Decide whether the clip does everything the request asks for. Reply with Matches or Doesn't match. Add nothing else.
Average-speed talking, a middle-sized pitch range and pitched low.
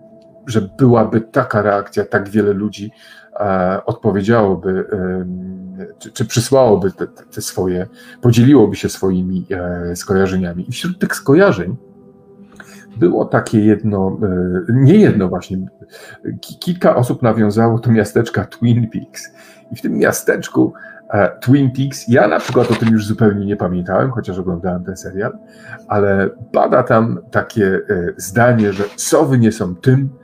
Matches